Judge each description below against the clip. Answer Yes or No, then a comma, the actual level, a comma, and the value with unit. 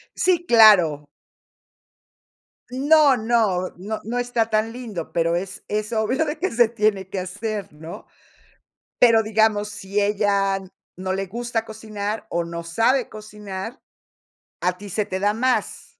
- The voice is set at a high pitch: Yes, high, 215 Hz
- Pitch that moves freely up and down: No, average, 3.3 semitones